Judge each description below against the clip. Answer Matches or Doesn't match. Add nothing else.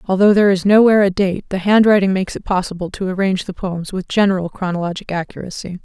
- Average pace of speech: Matches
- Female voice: Matches